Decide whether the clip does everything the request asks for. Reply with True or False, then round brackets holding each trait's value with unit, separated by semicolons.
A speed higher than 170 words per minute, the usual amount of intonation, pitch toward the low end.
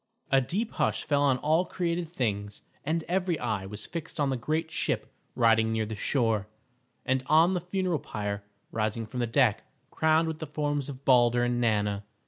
False (185 wpm; 6.3 semitones; 130 Hz)